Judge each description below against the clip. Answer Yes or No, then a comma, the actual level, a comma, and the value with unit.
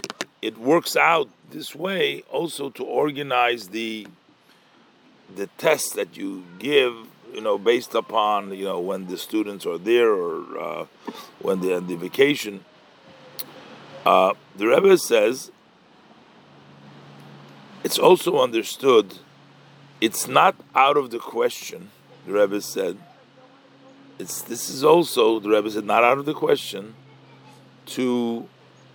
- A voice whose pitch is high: No, low, 130 Hz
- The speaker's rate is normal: No, slow, 125 wpm